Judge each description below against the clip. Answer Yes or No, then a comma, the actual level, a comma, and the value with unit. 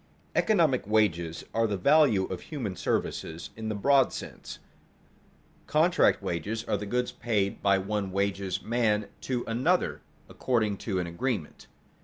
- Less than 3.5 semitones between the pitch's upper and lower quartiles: No, average, 4.1 semitones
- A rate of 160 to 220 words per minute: No, average, 140 wpm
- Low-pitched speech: Yes, low, 105 Hz